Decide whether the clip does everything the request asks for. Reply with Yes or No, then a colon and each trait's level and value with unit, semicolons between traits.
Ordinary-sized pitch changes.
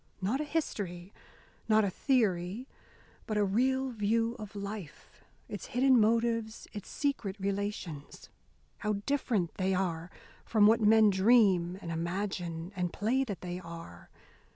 Yes: average, 4.1 semitones